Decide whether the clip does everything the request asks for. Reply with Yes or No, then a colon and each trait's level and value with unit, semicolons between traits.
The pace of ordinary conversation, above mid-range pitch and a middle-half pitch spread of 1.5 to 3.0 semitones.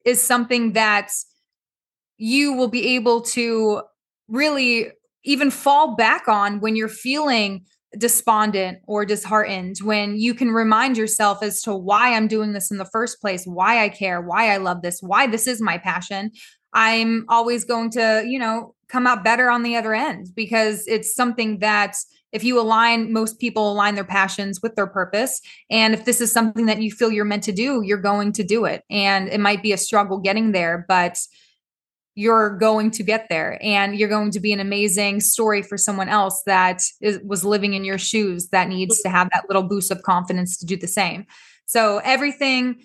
Yes: average, 195 wpm; high, 215 Hz; narrow, 2.4 semitones